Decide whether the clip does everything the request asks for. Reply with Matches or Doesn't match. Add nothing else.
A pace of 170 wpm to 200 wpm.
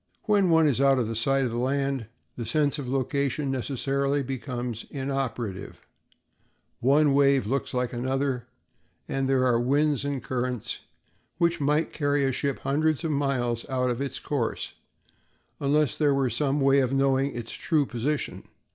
Doesn't match